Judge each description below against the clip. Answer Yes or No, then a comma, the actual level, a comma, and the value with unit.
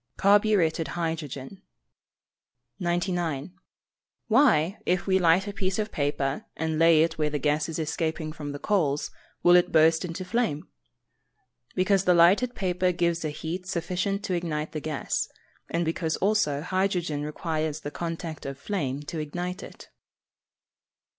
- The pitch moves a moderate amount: Yes, average, 3.2 semitones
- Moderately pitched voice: Yes, medium, 165 Hz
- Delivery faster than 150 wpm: No, average, 145 wpm